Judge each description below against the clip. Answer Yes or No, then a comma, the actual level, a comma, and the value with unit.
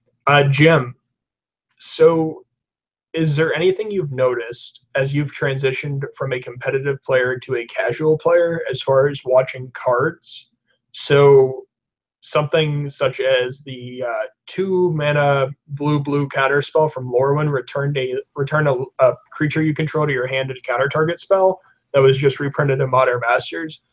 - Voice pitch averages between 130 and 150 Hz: Yes, medium, 140 Hz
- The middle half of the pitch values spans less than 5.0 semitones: Yes, average, 3.0 semitones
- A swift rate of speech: No, average, 155 wpm